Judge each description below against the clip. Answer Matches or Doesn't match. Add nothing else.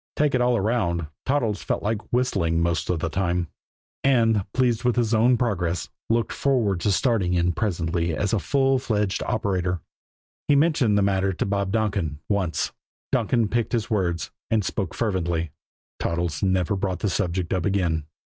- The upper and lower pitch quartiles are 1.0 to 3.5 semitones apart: Doesn't match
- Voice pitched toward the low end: Matches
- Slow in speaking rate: Doesn't match